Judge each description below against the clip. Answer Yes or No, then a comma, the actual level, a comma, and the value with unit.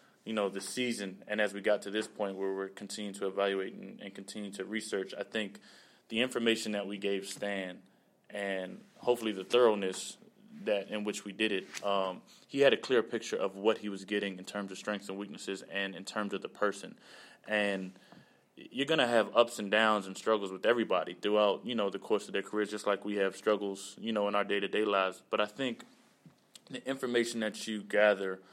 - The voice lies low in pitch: Yes, low, 100 Hz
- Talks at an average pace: No, fast, 215 wpm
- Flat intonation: Yes, narrow, 1.7 semitones